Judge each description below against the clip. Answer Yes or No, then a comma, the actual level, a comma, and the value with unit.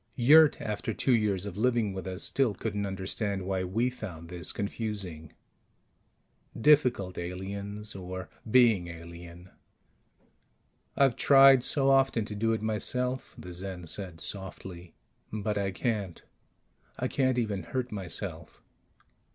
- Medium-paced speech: No, slow, 125 wpm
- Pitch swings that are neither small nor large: Yes, average, 4.4 semitones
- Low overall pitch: Yes, low, 100 Hz